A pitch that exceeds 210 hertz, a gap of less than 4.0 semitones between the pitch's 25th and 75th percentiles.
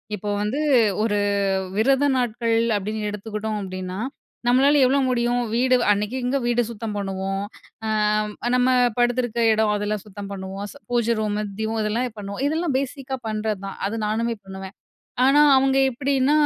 Yes: high, 220 Hz; average, 3.5 semitones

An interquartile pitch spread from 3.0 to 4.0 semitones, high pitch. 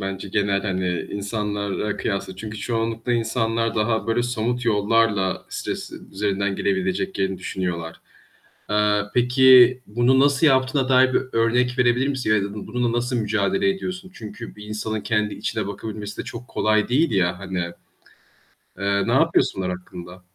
No: average, 3.7 semitones; low, 110 Hz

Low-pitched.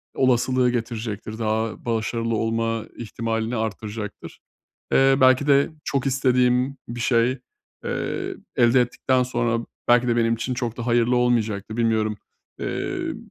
Yes: low, 120 Hz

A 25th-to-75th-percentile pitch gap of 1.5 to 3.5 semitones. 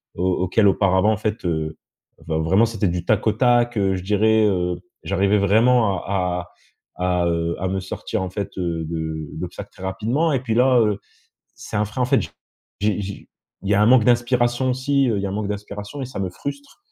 No: average, 4.4 semitones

